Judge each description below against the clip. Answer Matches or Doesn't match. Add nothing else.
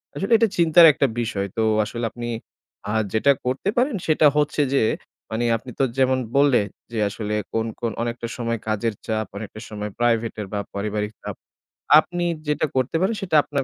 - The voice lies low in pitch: Matches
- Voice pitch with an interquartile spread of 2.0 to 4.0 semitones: Doesn't match